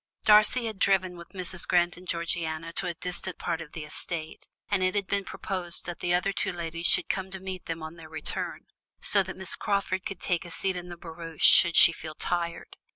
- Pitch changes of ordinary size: No, narrow, 2.1 semitones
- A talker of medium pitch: Yes, medium, 175 Hz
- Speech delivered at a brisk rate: Yes, fast, 220 wpm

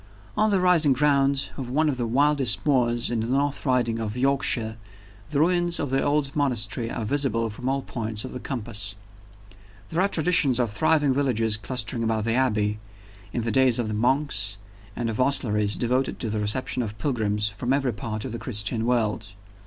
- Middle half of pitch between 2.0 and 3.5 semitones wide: No, average, 3.9 semitones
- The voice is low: Yes, low, 125 Hz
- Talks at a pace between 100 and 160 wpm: No, average, 190 wpm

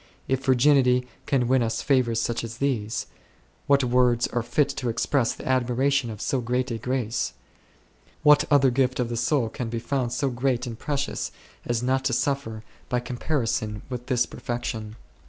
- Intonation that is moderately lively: No, narrow, 2.2 semitones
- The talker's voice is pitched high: No, low, 125 Hz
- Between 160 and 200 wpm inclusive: Yes, average, 175 wpm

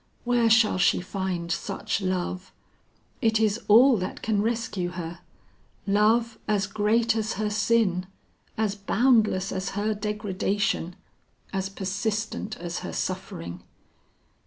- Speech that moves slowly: Yes, slow, 120 wpm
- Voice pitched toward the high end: Yes, high, 205 Hz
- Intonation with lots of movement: No, average, 2.8 semitones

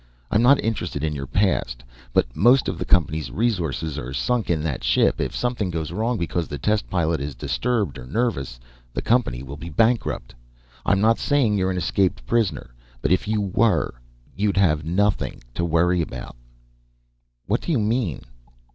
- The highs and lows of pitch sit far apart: Yes, wide, 6.7 semitones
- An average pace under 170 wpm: No, average, 175 wpm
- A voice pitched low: Yes, very low, 90 Hz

